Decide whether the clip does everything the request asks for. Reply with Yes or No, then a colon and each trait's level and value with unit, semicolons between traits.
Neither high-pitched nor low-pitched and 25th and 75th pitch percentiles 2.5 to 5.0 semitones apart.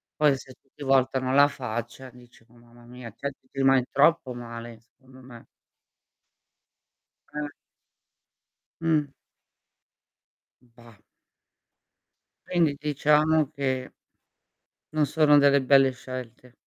No: low, 130 Hz; average, 2.8 semitones